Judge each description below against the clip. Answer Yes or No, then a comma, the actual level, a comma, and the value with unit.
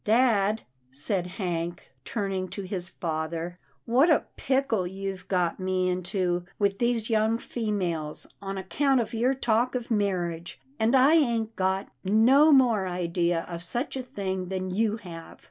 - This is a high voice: Yes, high, 195 Hz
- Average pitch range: Yes, average, 4.4 semitones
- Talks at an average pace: Yes, average, 160 wpm